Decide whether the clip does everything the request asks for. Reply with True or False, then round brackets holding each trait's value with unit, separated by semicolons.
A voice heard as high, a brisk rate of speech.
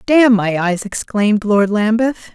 False (215 Hz; 155 wpm)